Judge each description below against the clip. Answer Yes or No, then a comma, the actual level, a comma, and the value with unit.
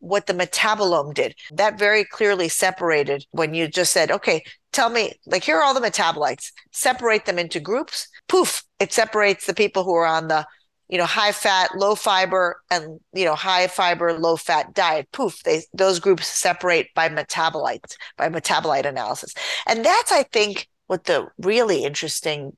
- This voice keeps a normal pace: Yes, average, 175 wpm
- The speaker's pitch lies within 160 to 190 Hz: Yes, medium, 185 Hz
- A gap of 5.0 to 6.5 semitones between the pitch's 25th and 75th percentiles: No, average, 4.1 semitones